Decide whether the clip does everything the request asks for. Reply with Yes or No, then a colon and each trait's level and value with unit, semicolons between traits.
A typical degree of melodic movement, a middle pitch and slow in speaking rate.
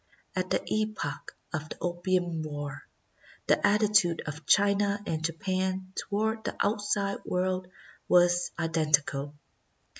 Yes: average, 4.0 semitones; medium, 180 Hz; slow, 120 wpm